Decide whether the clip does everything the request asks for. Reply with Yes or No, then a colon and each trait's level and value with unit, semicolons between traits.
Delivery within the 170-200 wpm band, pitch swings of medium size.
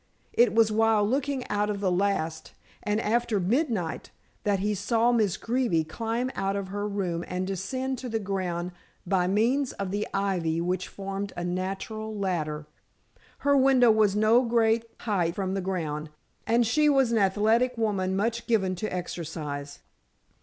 No: average, 160 wpm; average, 3.8 semitones